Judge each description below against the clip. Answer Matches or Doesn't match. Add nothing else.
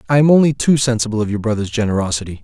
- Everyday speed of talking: Doesn't match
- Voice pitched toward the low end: Matches